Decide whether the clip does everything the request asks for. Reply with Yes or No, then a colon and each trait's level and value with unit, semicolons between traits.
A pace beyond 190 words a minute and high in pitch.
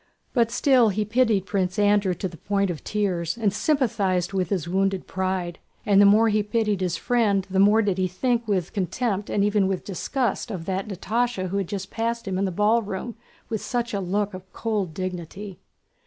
Yes: average, 200 wpm; high, 200 Hz